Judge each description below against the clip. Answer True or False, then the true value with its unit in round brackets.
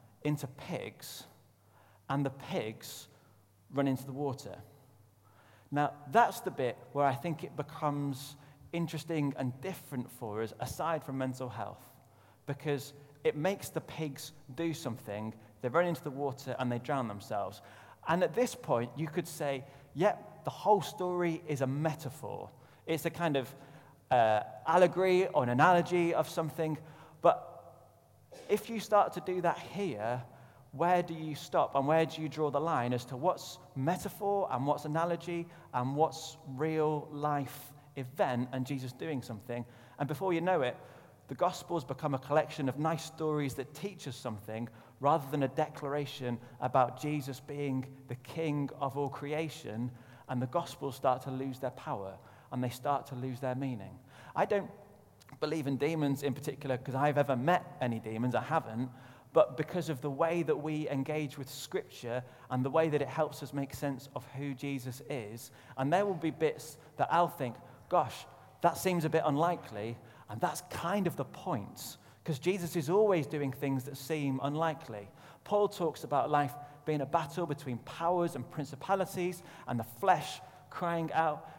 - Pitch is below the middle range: False (145 Hz)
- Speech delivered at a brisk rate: False (170 wpm)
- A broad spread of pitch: False (3.9 semitones)